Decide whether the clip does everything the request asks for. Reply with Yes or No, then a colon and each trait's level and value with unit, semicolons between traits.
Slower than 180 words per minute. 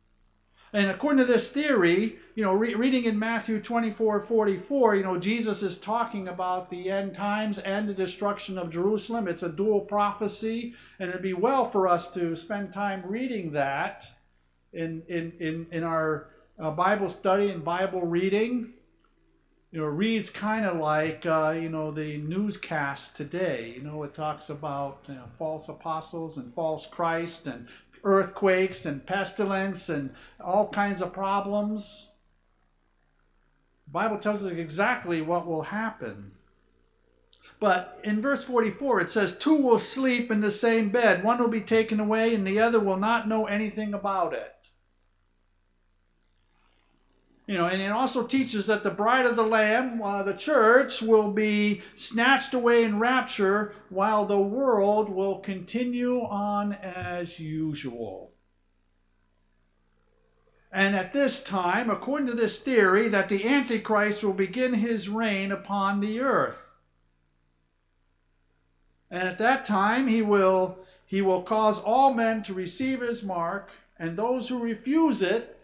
Yes: average, 150 wpm